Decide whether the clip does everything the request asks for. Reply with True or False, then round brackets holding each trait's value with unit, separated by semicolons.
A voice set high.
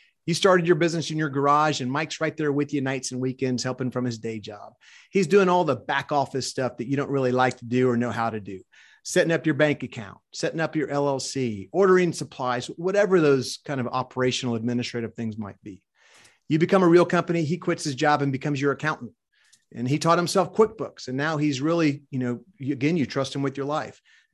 False (140 Hz)